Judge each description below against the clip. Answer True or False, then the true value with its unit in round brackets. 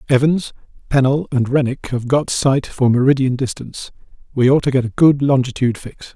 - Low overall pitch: True (130 Hz)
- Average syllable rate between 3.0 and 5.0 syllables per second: False (5.5 syllables/s)